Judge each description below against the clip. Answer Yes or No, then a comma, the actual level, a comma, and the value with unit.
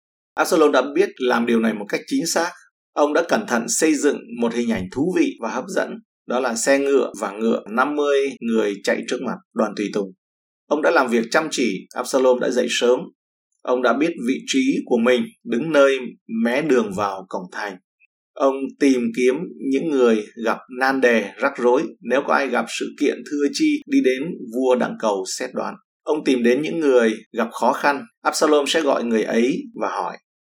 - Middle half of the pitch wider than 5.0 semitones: No, average, 3.8 semitones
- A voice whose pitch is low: Yes, low, 130 Hz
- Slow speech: No, average, 200 wpm